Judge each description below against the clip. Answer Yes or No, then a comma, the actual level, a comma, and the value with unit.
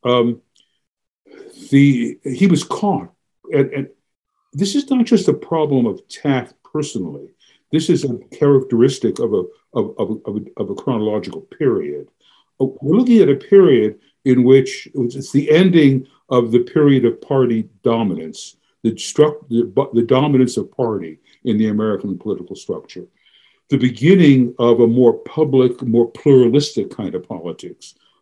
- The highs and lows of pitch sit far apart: Yes, wide, 5.7 semitones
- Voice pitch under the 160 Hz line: Yes, medium, 140 Hz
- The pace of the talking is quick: No, average, 150 wpm